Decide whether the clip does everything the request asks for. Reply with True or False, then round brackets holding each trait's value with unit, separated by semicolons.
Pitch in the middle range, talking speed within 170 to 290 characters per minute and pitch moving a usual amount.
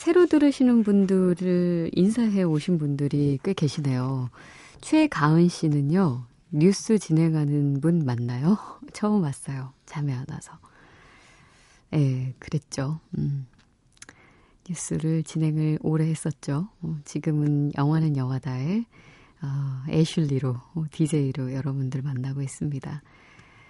True (155 Hz; 235 characters per minute; 3.9 semitones)